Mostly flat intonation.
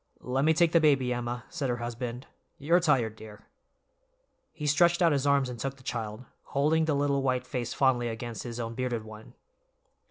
No: average, 3.4 semitones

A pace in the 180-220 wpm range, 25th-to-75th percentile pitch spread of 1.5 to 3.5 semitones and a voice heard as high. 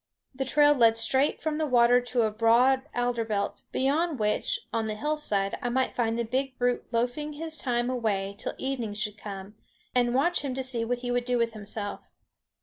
Yes: average, 200 wpm; average, 2.9 semitones; high, 245 Hz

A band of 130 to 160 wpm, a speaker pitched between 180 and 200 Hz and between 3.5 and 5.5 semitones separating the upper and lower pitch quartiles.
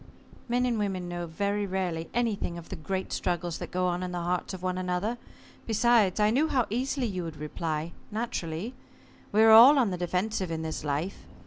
No: average, 200 wpm; medium, 185 Hz; average, 4.3 semitones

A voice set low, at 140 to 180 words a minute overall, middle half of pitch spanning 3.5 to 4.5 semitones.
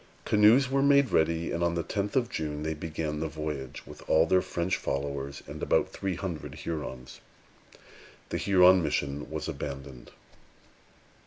Yes: very low, 80 Hz; average, 155 wpm; average, 4.2 semitones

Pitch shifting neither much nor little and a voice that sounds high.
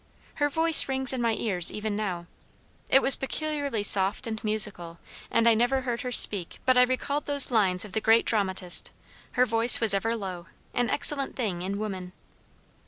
Yes: average, 4.7 semitones; high, 225 Hz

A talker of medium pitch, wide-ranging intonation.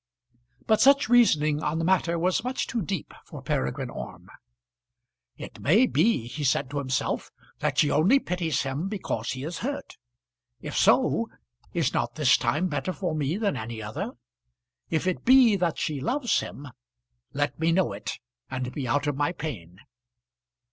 Yes: medium, 160 Hz; wide, 5.7 semitones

